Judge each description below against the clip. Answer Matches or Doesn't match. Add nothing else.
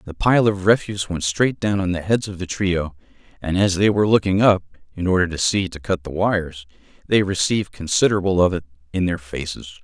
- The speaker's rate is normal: Doesn't match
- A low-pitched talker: Matches